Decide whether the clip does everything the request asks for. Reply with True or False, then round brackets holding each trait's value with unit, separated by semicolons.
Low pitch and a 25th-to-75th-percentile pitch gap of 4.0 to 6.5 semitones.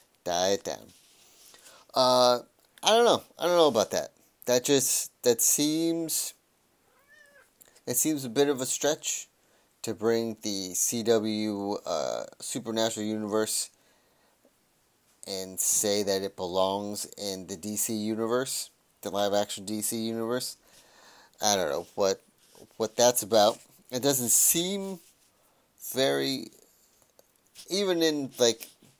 True (115 Hz; 4.4 semitones)